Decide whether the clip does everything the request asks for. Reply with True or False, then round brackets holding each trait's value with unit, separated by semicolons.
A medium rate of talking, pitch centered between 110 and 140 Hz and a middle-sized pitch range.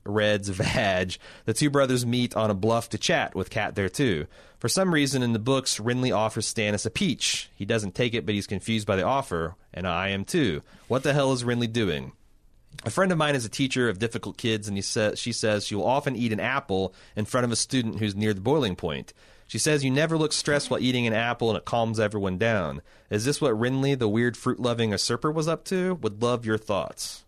False (240 wpm; 115 Hz; 3.8 semitones)